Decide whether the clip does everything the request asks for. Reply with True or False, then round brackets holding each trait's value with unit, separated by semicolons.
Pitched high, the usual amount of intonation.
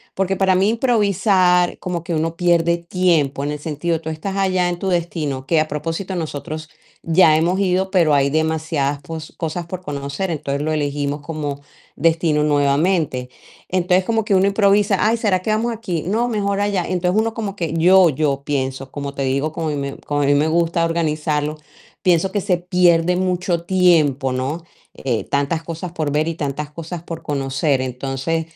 False (165 Hz; 3.9 semitones)